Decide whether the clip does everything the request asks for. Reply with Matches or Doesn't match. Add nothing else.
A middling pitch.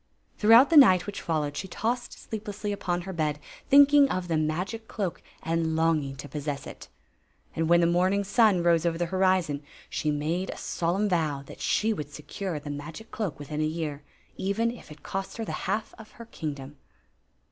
Matches